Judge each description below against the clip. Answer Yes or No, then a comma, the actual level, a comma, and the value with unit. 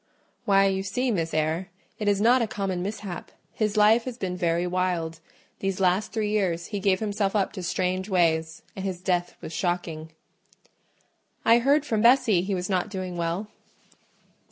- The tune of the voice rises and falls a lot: No, average, 3.0 semitones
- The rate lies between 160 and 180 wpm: Yes, average, 175 wpm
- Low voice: No, high, 190 Hz